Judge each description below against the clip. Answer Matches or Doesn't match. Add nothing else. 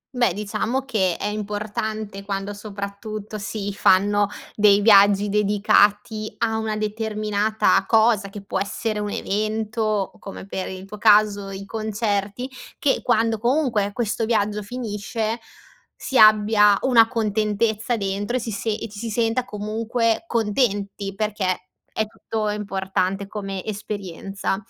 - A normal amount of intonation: Doesn't match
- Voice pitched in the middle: Doesn't match